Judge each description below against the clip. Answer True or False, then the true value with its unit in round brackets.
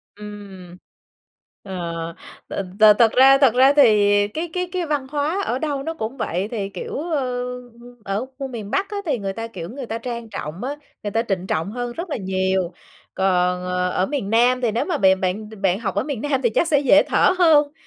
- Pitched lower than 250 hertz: True (230 Hz)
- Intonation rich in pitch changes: True (6.7 semitones)